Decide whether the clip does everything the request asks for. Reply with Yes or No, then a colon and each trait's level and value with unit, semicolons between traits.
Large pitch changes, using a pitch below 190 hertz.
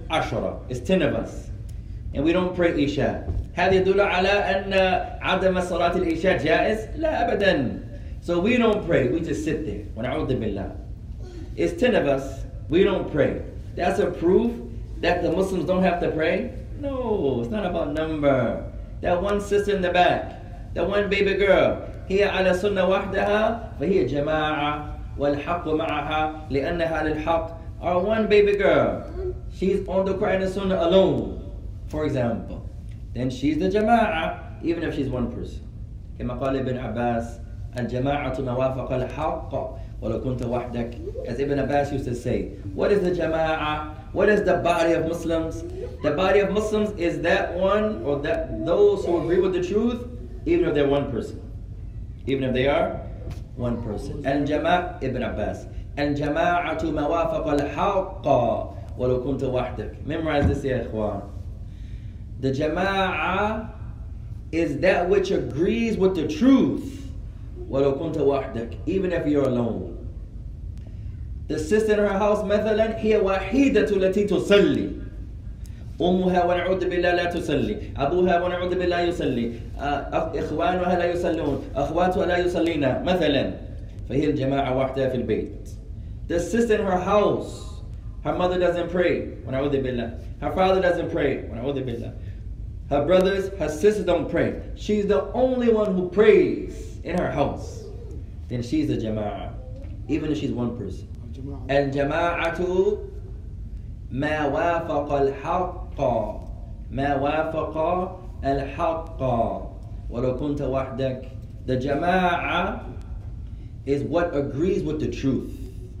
Yes: wide, 8.7 semitones; medium, 140 Hz